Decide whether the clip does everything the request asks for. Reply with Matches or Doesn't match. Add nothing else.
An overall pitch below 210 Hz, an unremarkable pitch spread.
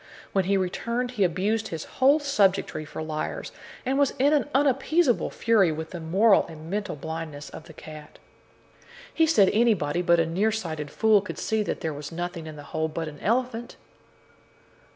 Doesn't match